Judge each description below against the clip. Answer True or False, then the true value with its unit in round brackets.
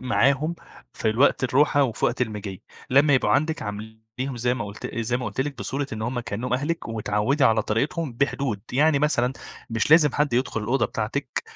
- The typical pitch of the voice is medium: False (125 Hz)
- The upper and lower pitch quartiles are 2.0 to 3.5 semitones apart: False (4.3 semitones)